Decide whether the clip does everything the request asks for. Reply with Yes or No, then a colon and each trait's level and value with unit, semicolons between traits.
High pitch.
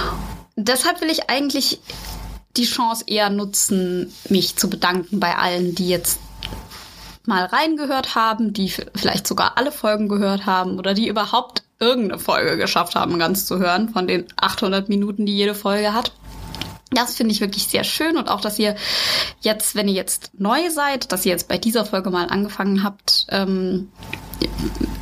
Yes: high, 205 Hz